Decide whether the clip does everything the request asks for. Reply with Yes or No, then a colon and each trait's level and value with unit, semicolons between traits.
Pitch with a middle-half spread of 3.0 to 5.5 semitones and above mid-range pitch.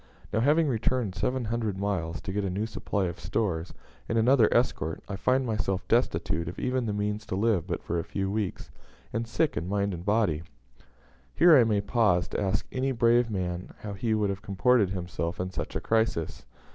No: average, 3.8 semitones; low, 105 Hz